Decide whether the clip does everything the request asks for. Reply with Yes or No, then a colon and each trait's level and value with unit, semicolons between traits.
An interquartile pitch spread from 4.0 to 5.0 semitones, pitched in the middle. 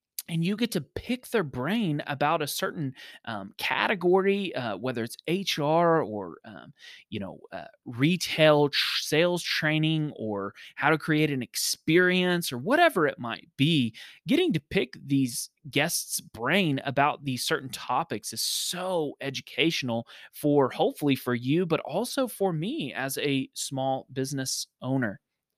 Yes: average, 4.7 semitones; medium, 150 Hz